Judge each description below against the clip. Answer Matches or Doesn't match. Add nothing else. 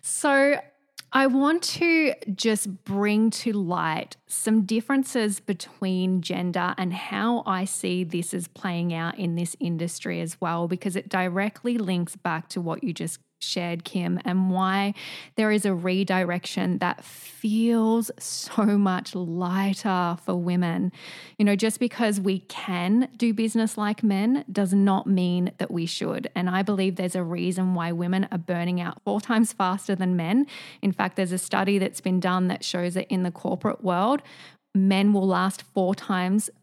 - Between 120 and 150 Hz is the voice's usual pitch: Doesn't match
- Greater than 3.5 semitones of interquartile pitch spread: Doesn't match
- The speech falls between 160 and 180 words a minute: Matches